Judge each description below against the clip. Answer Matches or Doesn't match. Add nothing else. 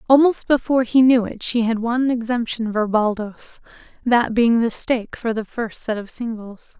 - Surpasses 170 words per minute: Matches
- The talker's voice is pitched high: Matches